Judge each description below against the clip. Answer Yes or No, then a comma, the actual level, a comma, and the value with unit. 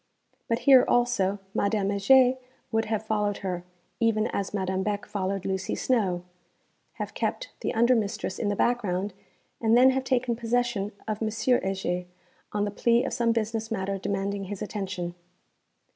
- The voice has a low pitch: No, high, 210 Hz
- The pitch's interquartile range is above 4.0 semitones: No, average, 3.3 semitones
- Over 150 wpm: Yes, average, 160 wpm